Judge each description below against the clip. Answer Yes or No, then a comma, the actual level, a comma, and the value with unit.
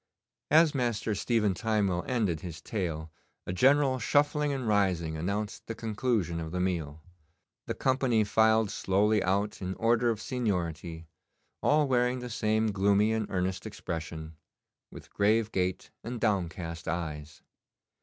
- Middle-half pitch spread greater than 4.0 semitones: Yes, average, 4.9 semitones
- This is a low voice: Yes, low, 105 Hz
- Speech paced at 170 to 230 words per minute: No, slow, 135 wpm